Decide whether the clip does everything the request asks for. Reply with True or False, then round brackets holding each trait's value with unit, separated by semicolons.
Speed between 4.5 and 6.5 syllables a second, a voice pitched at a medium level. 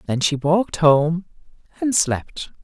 False (3.8 syllables/s; 165 Hz)